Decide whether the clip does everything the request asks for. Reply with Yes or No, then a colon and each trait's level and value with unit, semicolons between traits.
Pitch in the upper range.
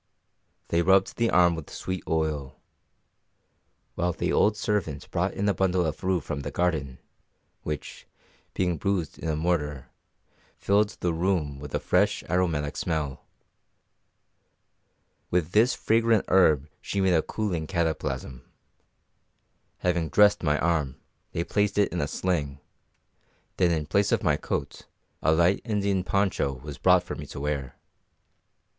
No: very low, 85 Hz